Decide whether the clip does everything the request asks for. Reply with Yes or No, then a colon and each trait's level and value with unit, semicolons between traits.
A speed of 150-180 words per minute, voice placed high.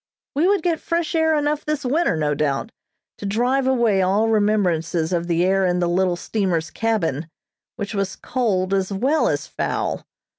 Yes: average, 175 wpm; high, 200 Hz